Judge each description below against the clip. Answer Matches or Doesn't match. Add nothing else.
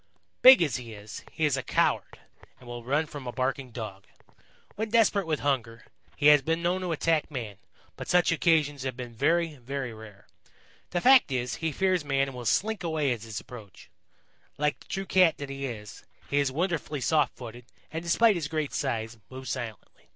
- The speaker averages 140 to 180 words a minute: Doesn't match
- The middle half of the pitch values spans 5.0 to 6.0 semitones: Matches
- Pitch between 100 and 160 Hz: Matches